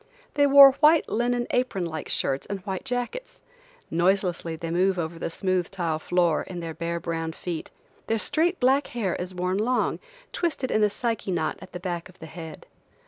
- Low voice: No, medium, 185 Hz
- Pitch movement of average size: No, wide, 6.4 semitones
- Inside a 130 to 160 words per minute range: No, average, 190 wpm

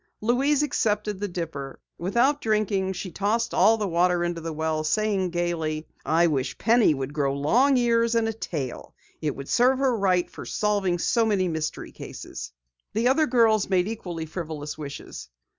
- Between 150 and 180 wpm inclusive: Yes, average, 170 wpm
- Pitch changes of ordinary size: No, wide, 5.9 semitones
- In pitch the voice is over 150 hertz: Yes, high, 190 Hz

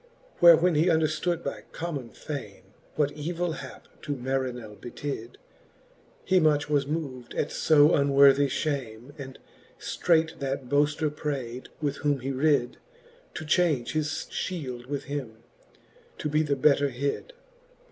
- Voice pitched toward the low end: No, medium, 145 Hz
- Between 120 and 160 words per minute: Yes, slow, 135 wpm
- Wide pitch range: No, average, 2.9 semitones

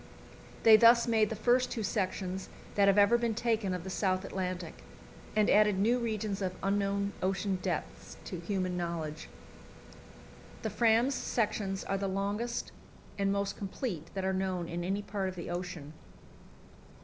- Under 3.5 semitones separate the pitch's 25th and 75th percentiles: Yes, average, 2.7 semitones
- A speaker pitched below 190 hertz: No, high, 195 Hz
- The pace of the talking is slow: No, average, 160 wpm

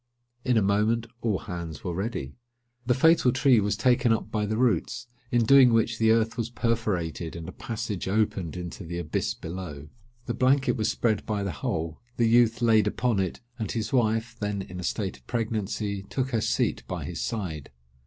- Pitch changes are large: No, average, 4.1 semitones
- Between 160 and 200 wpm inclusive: Yes, average, 195 wpm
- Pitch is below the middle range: Yes, low, 110 Hz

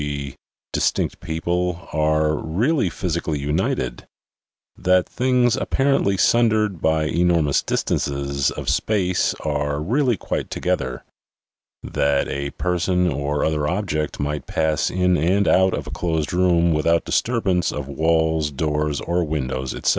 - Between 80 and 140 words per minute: Yes, slow, 135 wpm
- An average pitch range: Yes, average, 3.7 semitones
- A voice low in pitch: Yes, very low, 80 Hz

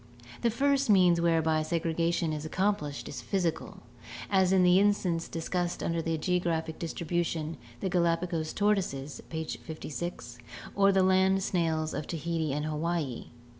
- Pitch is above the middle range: No, medium, 170 Hz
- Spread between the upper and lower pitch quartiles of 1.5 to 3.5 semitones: Yes, average, 2.8 semitones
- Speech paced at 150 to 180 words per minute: No, slow, 135 wpm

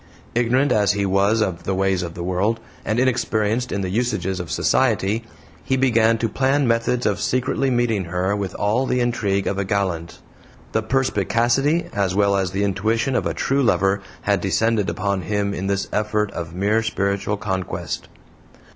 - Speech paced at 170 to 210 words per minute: Yes, average, 175 wpm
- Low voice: Yes, low, 105 Hz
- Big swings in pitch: No, average, 3.4 semitones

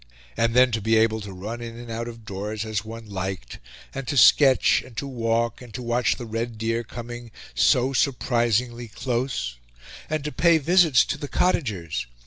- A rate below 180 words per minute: No, average, 185 wpm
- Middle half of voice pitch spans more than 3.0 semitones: No, narrow, 2.4 semitones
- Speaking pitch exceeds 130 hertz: No, low, 115 Hz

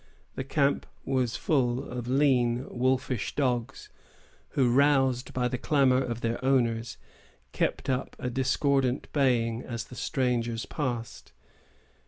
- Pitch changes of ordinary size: No, narrow, 2.0 semitones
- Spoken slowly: Yes, slow, 125 wpm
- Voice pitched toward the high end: No, low, 125 Hz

